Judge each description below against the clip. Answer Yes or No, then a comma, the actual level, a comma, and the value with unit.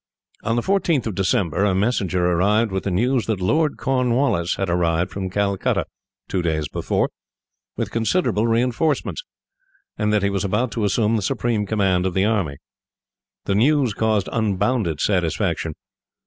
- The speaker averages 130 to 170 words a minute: Yes, average, 155 wpm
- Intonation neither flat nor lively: Yes, average, 4.1 semitones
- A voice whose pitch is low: Yes, low, 105 Hz